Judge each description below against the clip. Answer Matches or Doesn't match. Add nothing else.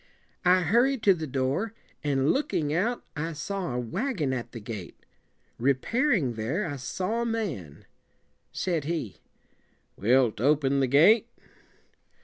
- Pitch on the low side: Doesn't match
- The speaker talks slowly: Doesn't match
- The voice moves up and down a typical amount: Doesn't match